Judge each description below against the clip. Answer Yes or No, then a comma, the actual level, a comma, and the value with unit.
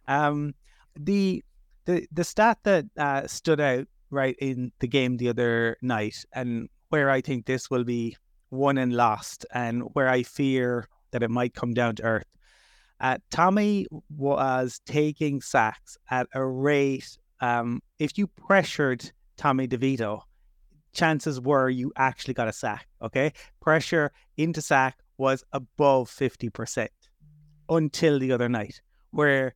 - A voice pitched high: No, low, 135 Hz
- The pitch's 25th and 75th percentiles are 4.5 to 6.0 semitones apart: No, average, 3.5 semitones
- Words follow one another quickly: No, average, 140 wpm